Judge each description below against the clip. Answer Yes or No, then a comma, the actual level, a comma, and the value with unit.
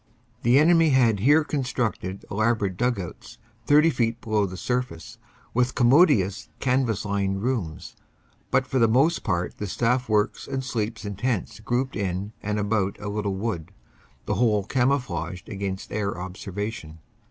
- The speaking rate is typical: Yes, average, 150 wpm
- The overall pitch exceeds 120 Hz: No, low, 110 Hz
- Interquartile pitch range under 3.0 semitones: No, average, 4.3 semitones